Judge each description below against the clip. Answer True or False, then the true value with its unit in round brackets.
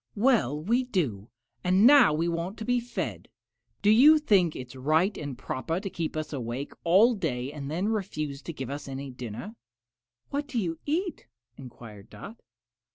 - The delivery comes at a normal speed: True (175 wpm)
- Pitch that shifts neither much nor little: False (8.0 semitones)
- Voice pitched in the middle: True (165 Hz)